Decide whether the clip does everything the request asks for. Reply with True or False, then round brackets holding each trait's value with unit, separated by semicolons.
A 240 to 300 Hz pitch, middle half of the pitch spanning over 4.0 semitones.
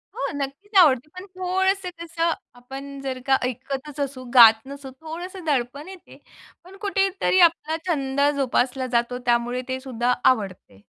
True (275 Hz; 5.1 semitones)